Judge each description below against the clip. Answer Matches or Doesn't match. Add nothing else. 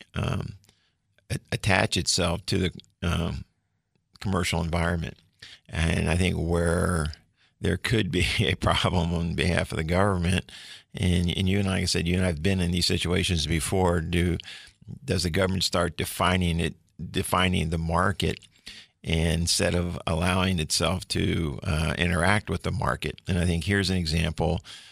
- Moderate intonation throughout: Doesn't match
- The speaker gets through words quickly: Doesn't match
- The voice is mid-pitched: Doesn't match